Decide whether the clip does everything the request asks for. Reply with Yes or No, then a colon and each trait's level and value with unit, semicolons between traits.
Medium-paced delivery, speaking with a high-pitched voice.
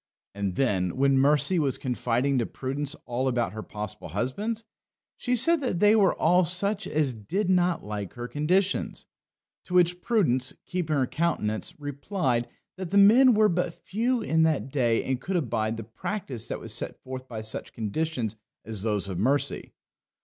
No: average, 170 wpm; medium, 140 Hz